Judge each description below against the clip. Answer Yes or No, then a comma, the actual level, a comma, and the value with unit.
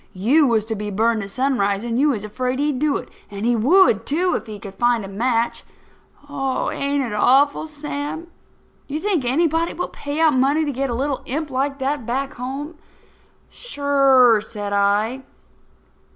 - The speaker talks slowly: No, average, 180 wpm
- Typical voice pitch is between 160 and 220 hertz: No, very high, 265 Hz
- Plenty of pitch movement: No, average, 4.3 semitones